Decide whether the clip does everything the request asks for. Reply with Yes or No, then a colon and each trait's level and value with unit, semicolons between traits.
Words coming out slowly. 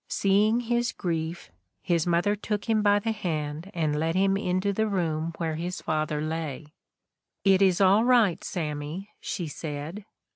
No: average, 160 wpm